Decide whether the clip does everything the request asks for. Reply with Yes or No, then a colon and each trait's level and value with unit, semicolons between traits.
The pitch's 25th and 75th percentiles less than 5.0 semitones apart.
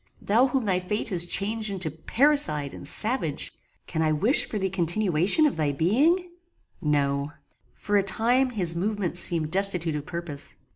No: wide, 5.4 semitones